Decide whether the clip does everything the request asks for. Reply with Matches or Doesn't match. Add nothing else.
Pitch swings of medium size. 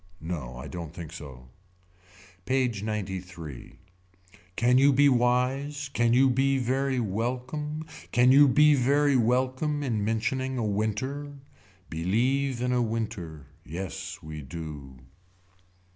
Doesn't match